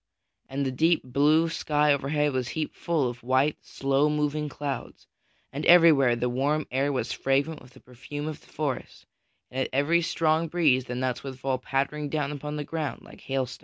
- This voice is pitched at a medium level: Yes, medium, 145 Hz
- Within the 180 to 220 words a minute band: Yes, average, 190 wpm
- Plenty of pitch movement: No, narrow, 2.6 semitones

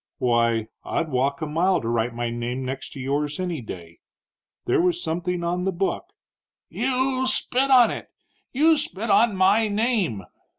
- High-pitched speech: No, medium, 175 Hz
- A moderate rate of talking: Yes, average, 170 wpm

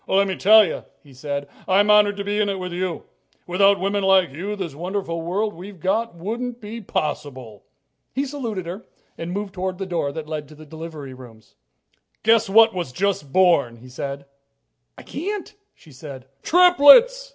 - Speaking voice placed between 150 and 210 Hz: Yes, medium, 185 Hz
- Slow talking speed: No, average, 180 wpm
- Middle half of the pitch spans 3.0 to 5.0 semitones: No, wide, 5.4 semitones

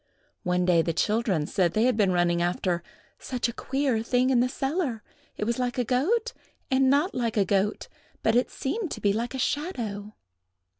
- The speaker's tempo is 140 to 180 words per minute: No, average, 195 wpm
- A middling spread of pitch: Yes, average, 4.9 semitones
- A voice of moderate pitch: No, high, 235 Hz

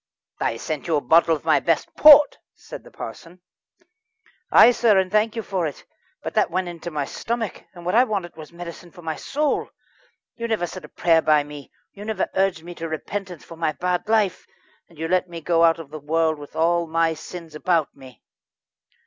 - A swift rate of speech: Yes, fast, 210 wpm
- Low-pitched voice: No, medium, 170 Hz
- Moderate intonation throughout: Yes, average, 3.2 semitones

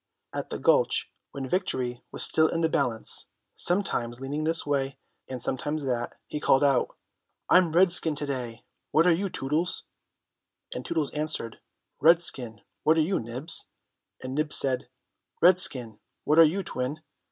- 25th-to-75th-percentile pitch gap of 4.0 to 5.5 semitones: Yes, average, 4.3 semitones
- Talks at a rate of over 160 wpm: No, average, 150 wpm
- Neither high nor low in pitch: Yes, medium, 150 Hz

